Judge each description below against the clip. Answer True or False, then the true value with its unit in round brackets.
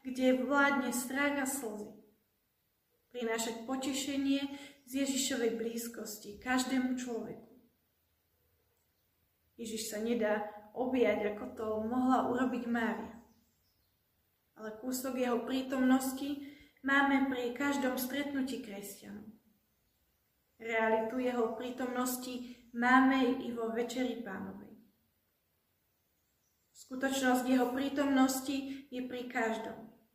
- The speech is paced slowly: True (85 wpm)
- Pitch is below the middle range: False (245 Hz)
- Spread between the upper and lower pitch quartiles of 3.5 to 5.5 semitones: False (2.8 semitones)